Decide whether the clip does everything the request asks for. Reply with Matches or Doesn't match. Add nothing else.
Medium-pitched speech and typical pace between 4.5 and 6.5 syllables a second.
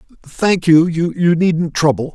Doesn't match